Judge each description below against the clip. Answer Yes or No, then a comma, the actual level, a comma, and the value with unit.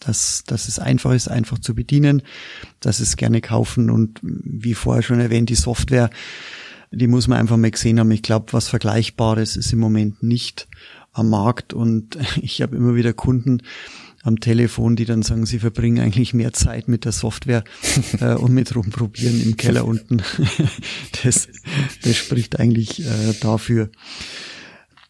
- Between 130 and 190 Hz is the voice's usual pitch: No, low, 115 Hz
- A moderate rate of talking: Yes, average, 160 wpm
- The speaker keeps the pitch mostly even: Yes, narrow, 1.3 semitones